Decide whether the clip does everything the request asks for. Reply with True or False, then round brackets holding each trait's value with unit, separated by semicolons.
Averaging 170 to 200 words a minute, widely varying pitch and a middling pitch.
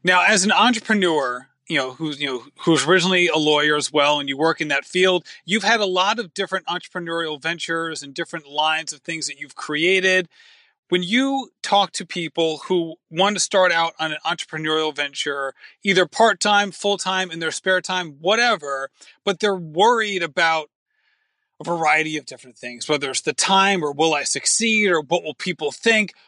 False (190 wpm; 4.4 semitones; 170 Hz)